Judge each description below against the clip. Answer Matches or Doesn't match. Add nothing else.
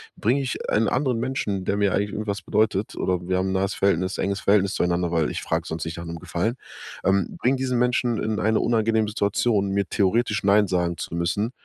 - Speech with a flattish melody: Doesn't match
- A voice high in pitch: Doesn't match